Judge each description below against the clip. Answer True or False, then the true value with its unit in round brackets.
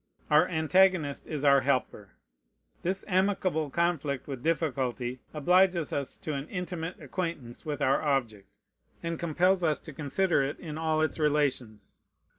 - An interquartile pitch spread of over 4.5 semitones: False (3.7 semitones)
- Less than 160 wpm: True (140 wpm)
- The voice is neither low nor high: True (155 Hz)